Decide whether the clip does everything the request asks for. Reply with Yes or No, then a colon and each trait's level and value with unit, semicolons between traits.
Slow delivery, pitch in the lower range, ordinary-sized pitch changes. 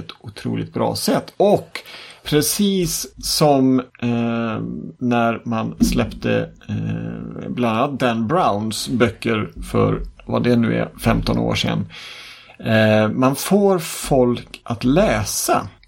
Yes: slow, 115 wpm; low, 120 Hz; average, 3.4 semitones